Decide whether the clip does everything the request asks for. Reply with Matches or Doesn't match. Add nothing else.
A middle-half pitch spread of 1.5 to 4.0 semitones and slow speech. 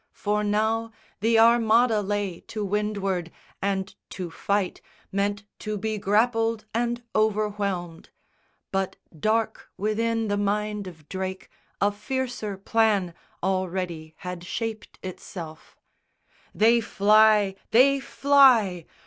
Matches